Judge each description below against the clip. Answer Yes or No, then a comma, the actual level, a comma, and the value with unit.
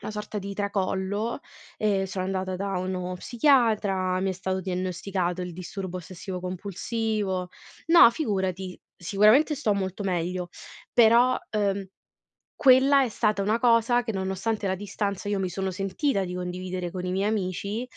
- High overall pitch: Yes, high, 195 Hz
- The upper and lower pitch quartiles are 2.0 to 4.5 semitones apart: Yes, average, 2.7 semitones